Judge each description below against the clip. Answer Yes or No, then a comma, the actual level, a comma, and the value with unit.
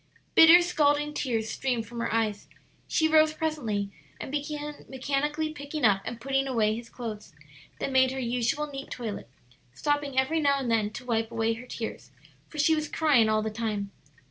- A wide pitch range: No, average, 4.7 semitones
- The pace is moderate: Yes, average, 180 wpm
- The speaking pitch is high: Yes, very high, 260 Hz